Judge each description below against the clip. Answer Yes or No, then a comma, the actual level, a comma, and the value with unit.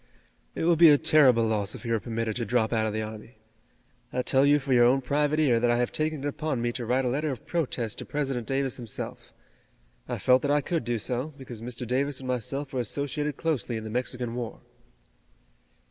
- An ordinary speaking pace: No, fast, 225 wpm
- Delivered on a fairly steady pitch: No, average, 3.5 semitones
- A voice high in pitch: No, low, 125 Hz